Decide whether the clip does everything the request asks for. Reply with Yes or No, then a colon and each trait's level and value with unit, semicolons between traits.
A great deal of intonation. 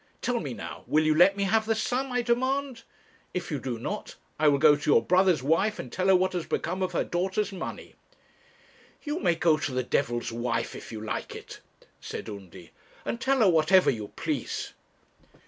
Yes: wide, 7.4 semitones